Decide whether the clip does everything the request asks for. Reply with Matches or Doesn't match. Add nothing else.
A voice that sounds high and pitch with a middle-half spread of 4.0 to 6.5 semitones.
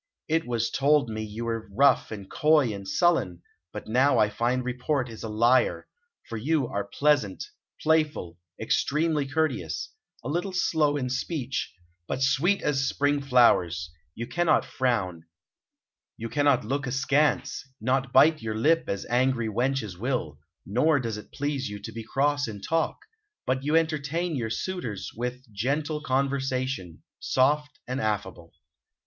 Doesn't match